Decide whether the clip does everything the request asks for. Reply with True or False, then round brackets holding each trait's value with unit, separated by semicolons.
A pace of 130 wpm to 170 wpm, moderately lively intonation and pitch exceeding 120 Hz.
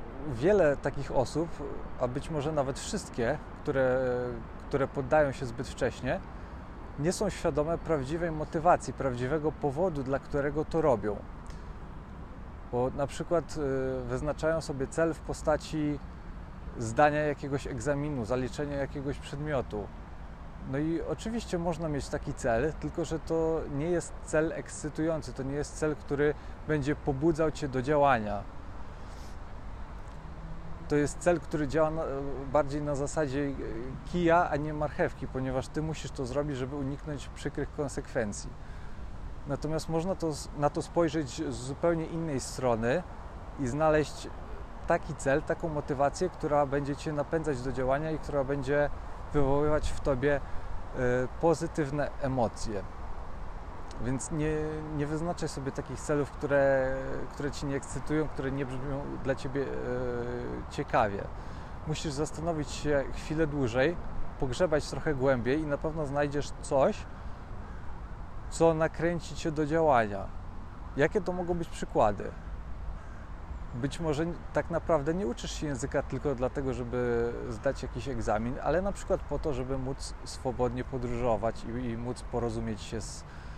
True (135 wpm; 3.8 semitones; 140 Hz)